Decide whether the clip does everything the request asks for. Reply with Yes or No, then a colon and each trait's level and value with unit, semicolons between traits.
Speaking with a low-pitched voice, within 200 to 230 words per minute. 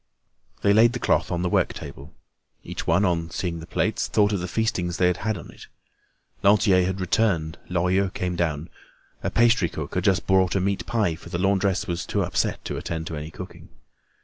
Yes: very low, 90 Hz; fast, 205 wpm